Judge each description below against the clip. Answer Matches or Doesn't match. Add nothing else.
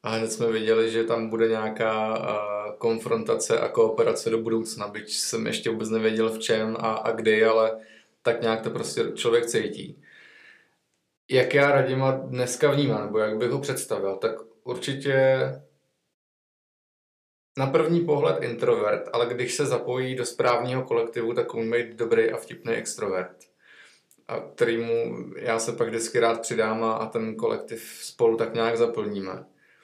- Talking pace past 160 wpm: Doesn't match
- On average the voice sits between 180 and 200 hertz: Doesn't match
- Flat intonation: Doesn't match